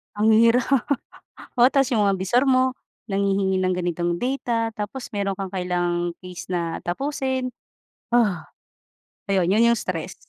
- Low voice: No, high, 200 Hz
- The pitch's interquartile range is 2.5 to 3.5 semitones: No, average, 5.1 semitones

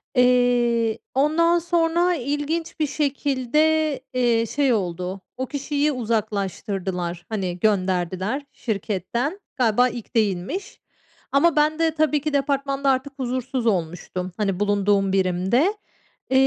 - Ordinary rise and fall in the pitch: No, wide, 6.6 semitones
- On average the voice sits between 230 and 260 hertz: Yes, very high, 250 Hz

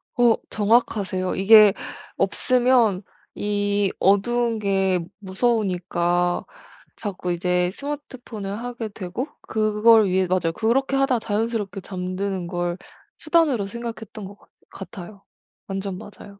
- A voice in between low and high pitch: No, high, 205 Hz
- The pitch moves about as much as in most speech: Yes, average, 3.7 semitones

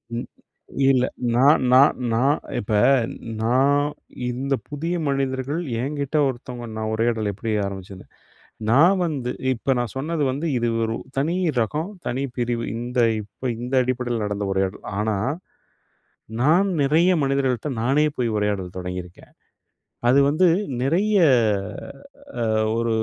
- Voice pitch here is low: Yes, low, 130 Hz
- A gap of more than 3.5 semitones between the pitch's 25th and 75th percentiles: Yes, average, 4.1 semitones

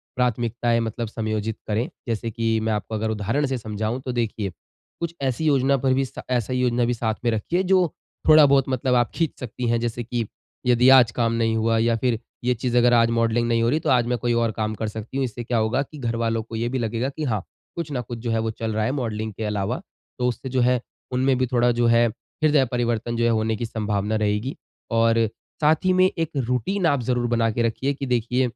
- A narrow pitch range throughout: Yes, narrow, 2.3 semitones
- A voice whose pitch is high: No, low, 120 Hz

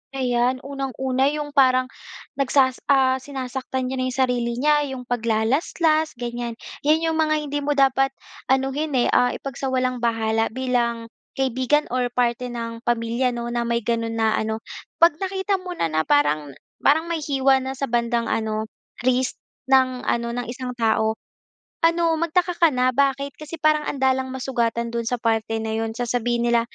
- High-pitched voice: Yes, very high, 255 Hz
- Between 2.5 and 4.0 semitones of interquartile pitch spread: Yes, average, 2.8 semitones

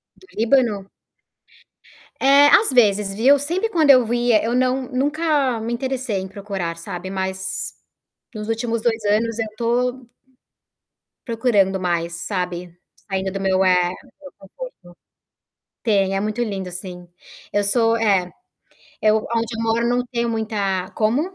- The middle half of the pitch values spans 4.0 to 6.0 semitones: Yes, average, 4.3 semitones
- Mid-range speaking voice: No, high, 225 Hz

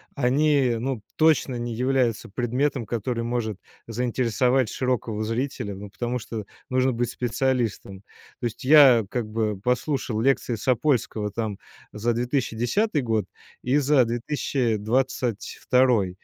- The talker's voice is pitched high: No, low, 120 Hz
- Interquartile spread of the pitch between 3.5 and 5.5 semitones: No, average, 2.7 semitones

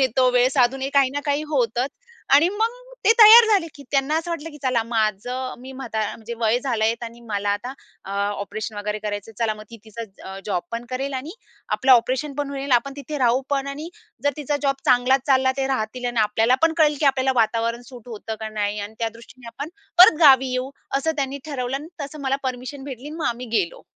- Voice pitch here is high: Yes, very high, 255 Hz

